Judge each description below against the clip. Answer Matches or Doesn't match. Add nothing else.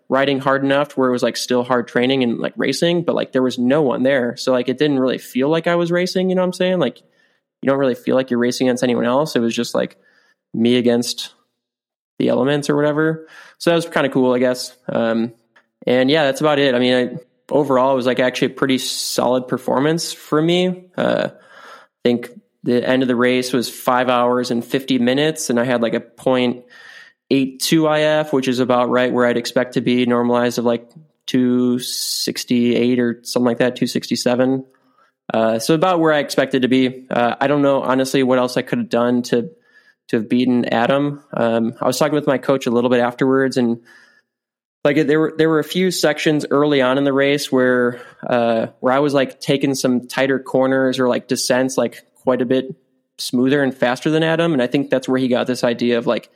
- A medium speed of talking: Doesn't match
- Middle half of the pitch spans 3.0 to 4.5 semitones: Doesn't match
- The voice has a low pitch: Matches